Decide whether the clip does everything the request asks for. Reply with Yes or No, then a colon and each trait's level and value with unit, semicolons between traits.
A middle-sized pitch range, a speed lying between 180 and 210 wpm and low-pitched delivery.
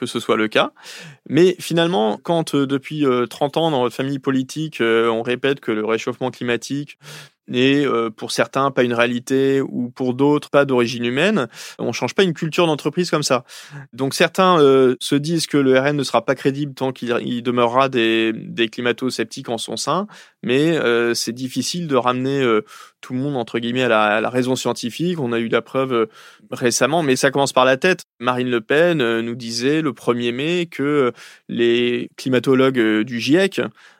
Yes: average, 3.2 semitones; average, 195 wpm; low, 130 Hz